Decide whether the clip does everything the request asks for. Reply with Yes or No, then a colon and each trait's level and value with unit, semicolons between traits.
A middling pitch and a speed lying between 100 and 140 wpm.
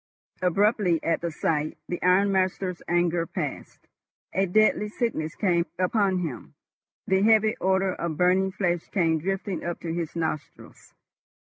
Yes: medium, 180 Hz; slow, 135 wpm